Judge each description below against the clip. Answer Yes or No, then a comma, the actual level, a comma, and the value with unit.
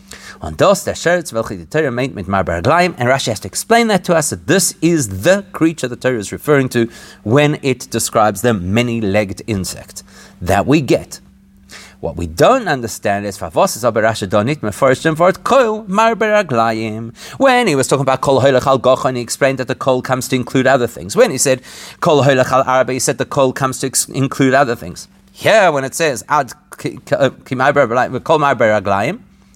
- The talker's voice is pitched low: Yes, low, 130 Hz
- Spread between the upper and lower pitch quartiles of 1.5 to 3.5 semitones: No, average, 4.7 semitones